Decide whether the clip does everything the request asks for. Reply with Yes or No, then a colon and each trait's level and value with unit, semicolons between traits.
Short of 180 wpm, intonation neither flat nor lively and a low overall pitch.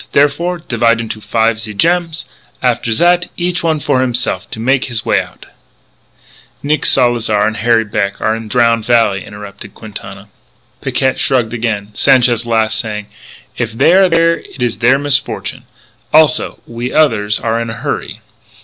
Yes: average, 165 wpm; average, 4.0 semitones; low, 115 Hz